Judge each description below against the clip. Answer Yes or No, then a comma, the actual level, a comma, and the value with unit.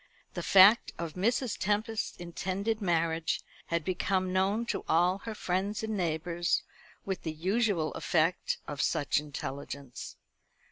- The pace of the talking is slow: Yes, slow, 130 wpm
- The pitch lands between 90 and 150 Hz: No, medium, 185 Hz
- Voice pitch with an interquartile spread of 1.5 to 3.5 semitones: No, average, 3.9 semitones